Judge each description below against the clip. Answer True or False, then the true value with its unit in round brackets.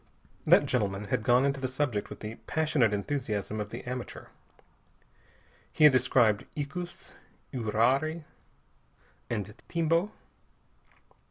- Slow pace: True (110 wpm)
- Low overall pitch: True (125 Hz)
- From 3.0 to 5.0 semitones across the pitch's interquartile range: False (5.5 semitones)